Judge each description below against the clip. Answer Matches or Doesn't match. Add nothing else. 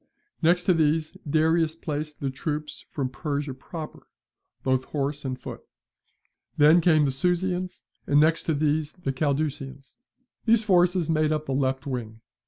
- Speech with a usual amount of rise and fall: Matches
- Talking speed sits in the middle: Matches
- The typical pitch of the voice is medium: Matches